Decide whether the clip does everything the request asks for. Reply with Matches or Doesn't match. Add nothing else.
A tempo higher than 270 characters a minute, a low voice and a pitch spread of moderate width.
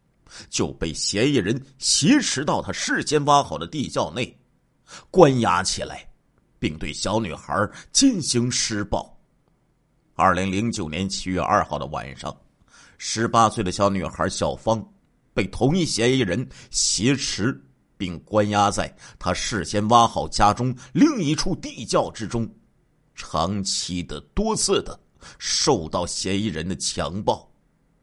Doesn't match